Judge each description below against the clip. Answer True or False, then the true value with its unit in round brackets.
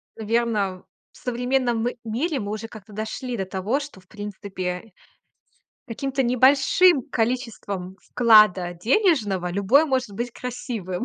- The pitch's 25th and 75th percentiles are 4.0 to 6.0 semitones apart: True (4.4 semitones)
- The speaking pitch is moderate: False (225 Hz)